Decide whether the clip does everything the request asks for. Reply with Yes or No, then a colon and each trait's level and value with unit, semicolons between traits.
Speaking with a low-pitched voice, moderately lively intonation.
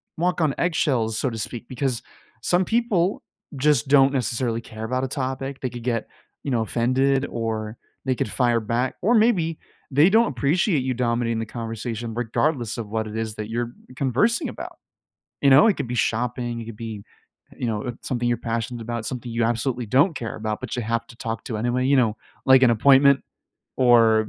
Yes: low, 120 Hz; average, 3.1 semitones